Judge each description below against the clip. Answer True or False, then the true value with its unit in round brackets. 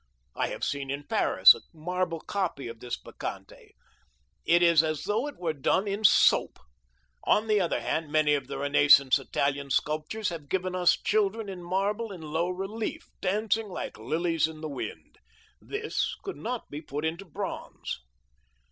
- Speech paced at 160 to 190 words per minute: True (165 wpm)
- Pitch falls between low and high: True (170 Hz)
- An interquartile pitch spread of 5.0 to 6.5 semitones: True (5.3 semitones)